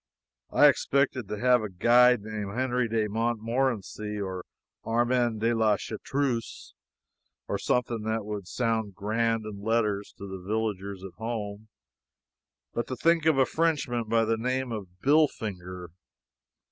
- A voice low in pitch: Yes, low, 115 Hz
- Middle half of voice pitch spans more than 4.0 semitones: No, average, 3.0 semitones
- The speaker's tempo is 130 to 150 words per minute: Yes, average, 140 wpm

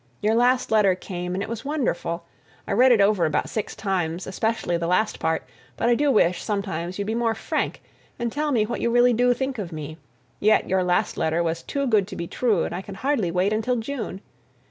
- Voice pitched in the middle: No, high, 210 Hz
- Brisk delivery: Yes, fast, 225 wpm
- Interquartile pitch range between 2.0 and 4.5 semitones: No, average, 5.0 semitones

